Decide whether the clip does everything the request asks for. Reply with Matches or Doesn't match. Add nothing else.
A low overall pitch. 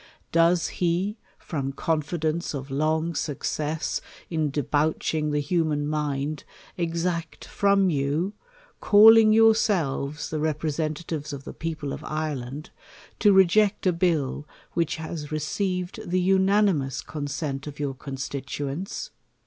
Doesn't match